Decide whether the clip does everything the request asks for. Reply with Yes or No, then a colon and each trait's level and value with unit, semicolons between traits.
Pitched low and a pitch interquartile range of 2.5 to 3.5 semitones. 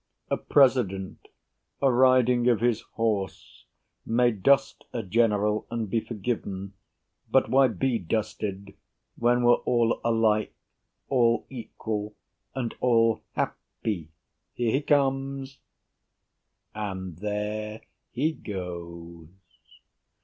Yes: low, 115 Hz; average, 3.2 semitones